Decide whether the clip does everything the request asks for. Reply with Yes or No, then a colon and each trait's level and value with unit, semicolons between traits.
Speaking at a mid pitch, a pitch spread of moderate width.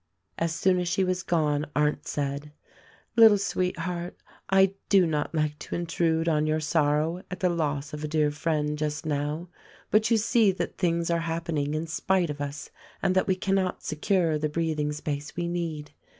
Yes: medium, 165 Hz; average, 3.3 semitones